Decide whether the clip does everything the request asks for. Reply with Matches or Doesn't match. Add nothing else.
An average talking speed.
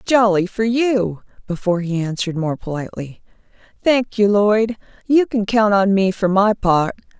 Matches